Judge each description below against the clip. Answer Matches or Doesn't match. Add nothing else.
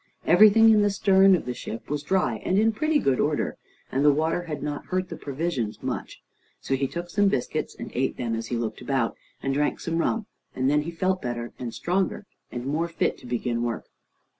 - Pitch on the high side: Doesn't match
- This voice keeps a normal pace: Doesn't match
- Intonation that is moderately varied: Doesn't match